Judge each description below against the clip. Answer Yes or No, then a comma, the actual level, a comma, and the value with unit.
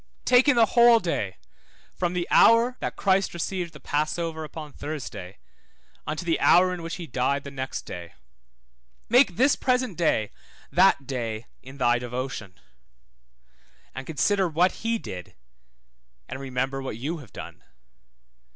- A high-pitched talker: No, medium, 155 Hz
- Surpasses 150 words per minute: No, average, 145 wpm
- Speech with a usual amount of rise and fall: No, wide, 6.2 semitones